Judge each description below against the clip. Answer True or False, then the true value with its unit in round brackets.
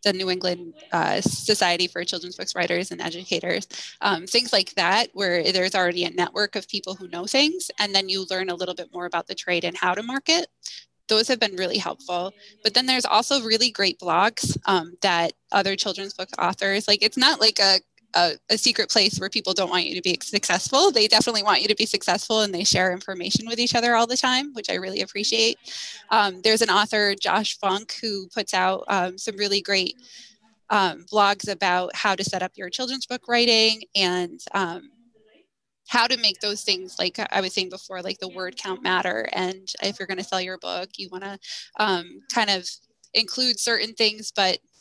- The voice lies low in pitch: False (195 Hz)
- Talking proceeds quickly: True (210 wpm)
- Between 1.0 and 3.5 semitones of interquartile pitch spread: True (3.1 semitones)